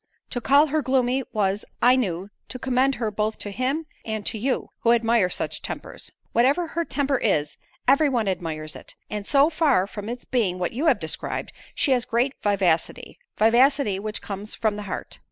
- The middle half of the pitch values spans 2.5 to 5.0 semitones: Yes, average, 4.7 semitones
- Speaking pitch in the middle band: No, high, 235 Hz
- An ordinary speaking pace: Yes, average, 190 wpm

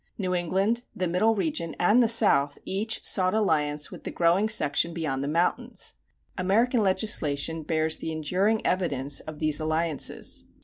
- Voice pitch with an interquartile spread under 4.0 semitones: No, average, 5.2 semitones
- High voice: No, medium, 175 Hz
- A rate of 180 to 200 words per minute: No, average, 150 wpm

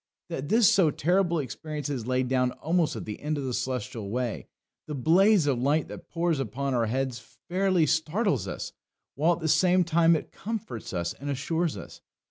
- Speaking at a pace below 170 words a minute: No, average, 190 wpm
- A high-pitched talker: No, medium, 150 Hz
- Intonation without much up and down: No, average, 5.1 semitones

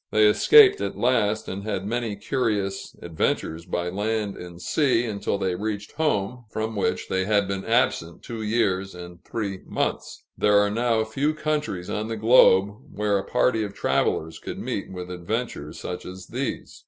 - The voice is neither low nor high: No, low, 105 Hz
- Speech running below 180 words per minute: Yes, average, 170 wpm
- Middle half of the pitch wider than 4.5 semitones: No, average, 3.4 semitones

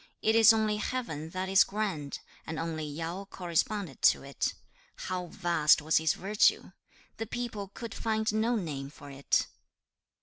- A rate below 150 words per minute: No, average, 155 wpm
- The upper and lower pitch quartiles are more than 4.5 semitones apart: Yes, wide, 5.5 semitones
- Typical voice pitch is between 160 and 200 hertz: Yes, medium, 185 Hz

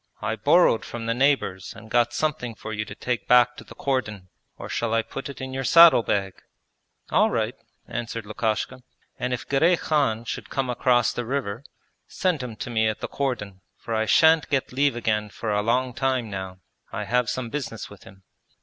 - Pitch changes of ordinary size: Yes, average, 3.3 semitones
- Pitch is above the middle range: No, low, 120 Hz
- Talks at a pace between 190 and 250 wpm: Yes, average, 200 wpm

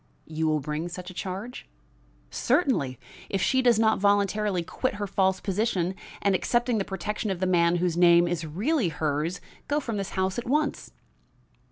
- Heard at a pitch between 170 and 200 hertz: Yes, high, 190 Hz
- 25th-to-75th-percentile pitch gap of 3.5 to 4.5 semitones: Yes, average, 4.1 semitones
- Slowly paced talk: No, average, 175 wpm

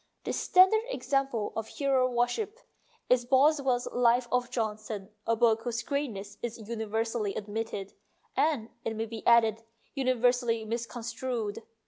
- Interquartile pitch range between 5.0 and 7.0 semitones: No, narrow, 2.5 semitones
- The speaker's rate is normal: No, slow, 130 wpm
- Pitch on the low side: No, high, 235 Hz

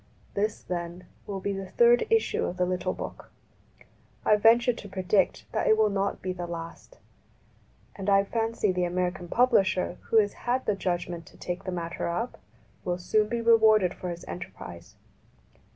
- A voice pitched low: No, high, 190 Hz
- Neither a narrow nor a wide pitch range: Yes, average, 3.5 semitones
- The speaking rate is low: No, average, 175 wpm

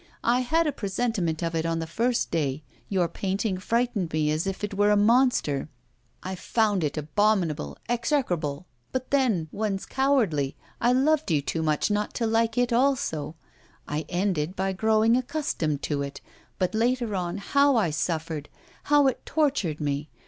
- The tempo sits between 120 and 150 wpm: No, average, 165 wpm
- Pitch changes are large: Yes, wide, 7.1 semitones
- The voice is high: Yes, high, 195 Hz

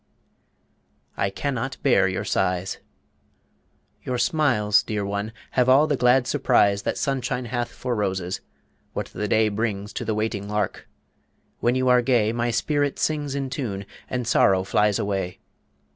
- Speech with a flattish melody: No, average, 4.1 semitones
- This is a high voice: No, low, 115 Hz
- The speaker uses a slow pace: No, average, 155 wpm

